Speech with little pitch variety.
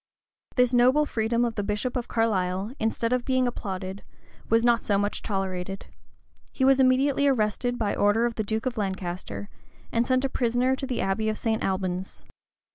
No: average, 4.0 semitones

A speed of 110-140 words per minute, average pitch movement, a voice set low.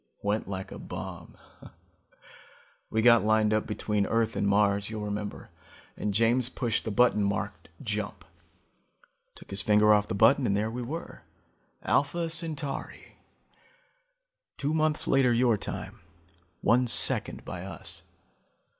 Yes: slow, 135 wpm; average, 3.4 semitones; low, 110 Hz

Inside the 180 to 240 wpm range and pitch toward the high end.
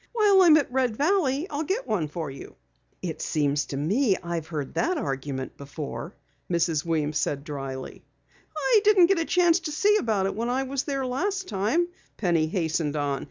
Yes: average, 185 wpm; high, 210 Hz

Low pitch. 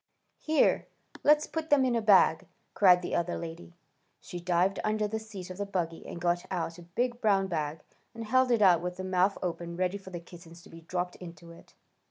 No: medium, 180 Hz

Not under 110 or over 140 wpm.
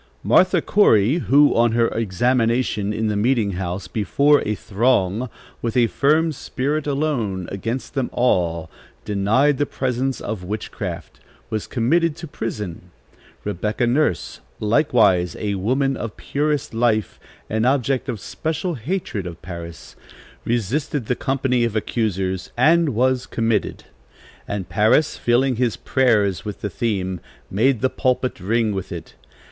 Yes: slow, 135 wpm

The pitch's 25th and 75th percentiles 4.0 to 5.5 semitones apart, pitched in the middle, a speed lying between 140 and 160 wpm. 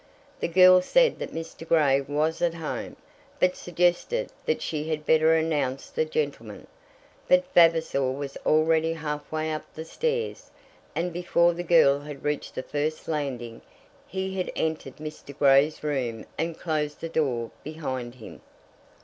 No: average, 2.9 semitones; medium, 155 Hz; average, 150 wpm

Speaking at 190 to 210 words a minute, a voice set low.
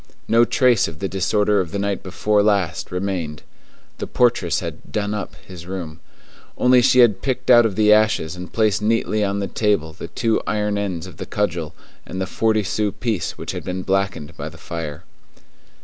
Yes: average, 195 wpm; low, 100 Hz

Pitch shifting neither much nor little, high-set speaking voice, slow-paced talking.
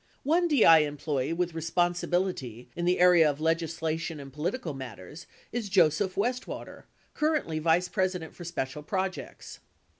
No: average, 3.5 semitones; medium, 165 Hz; slow, 130 wpm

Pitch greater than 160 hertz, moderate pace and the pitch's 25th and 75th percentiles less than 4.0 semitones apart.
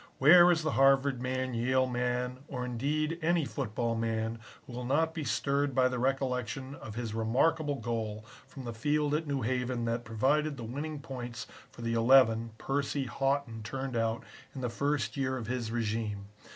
No: low, 130 Hz; average, 180 wpm; average, 3.3 semitones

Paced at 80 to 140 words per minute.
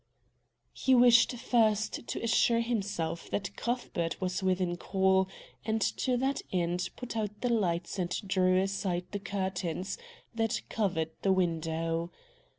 Yes: slow, 135 wpm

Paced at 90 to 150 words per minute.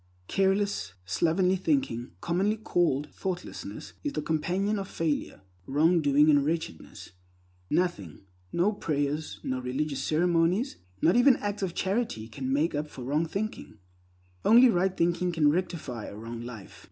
Yes: average, 140 wpm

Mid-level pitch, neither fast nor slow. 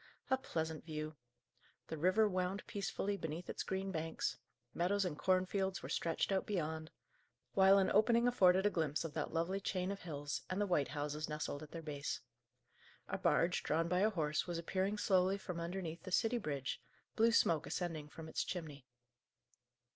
Yes: medium, 175 Hz; average, 175 wpm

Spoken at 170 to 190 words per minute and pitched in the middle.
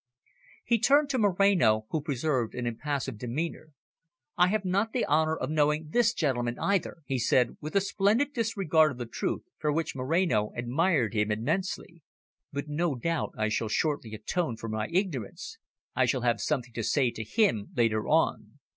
Yes: average, 175 wpm; medium, 150 Hz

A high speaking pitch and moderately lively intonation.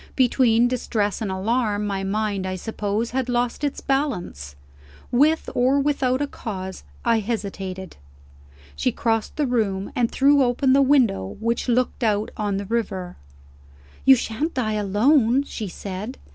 Yes: high, 225 Hz; average, 4.4 semitones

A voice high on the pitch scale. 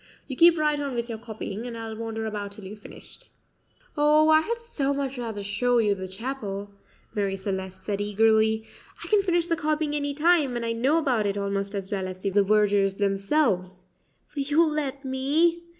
Yes: high, 230 Hz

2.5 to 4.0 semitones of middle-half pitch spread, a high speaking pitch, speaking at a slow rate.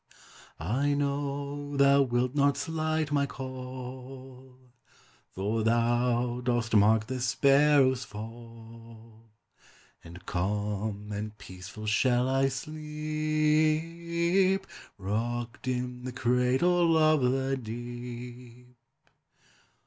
No: average, 3.6 semitones; low, 125 Hz; slow, 90 wpm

